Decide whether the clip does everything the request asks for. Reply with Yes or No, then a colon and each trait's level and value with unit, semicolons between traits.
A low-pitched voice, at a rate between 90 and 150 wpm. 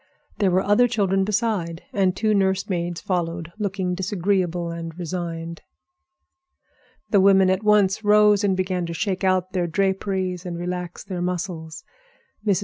No: medium, 185 Hz; average, 145 wpm